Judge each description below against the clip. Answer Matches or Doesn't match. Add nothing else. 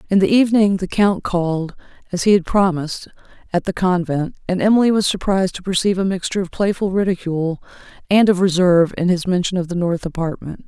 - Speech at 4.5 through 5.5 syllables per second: Doesn't match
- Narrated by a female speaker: Matches